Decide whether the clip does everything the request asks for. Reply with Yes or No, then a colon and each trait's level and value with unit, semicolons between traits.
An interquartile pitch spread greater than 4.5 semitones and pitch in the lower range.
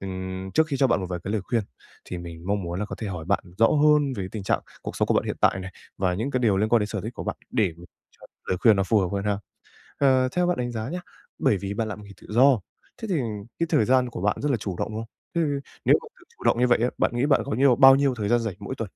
Yes: average, 5.2 semitones; low, 110 Hz